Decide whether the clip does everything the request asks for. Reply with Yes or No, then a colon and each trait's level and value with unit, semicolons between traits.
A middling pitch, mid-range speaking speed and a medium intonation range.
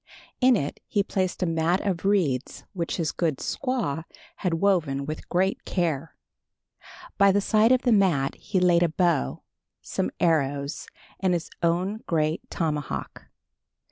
Yes: medium, 175 Hz; average, 145 wpm; average, 4.1 semitones